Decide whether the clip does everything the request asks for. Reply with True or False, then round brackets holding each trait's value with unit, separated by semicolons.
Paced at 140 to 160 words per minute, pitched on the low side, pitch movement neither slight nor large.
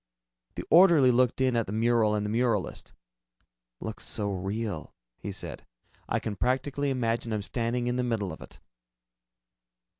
True (155 wpm; 115 Hz; 3.1 semitones)